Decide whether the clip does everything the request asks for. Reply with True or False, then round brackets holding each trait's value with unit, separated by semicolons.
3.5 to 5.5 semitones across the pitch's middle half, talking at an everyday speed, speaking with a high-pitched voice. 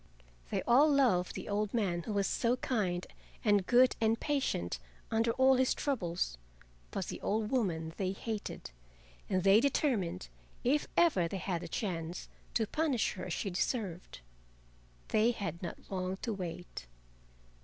True (5.2 semitones; 155 wpm; 205 Hz)